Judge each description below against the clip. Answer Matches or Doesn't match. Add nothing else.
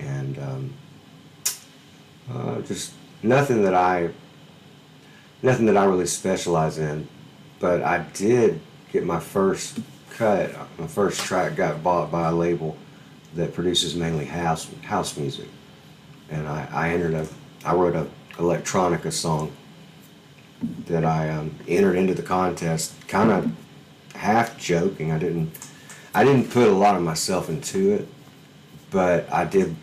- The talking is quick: Doesn't match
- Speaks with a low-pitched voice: Matches